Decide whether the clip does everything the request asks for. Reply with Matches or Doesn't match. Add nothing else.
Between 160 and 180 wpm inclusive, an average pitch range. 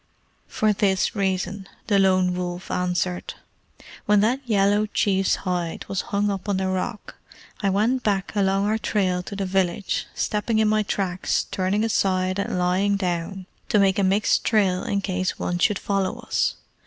Doesn't match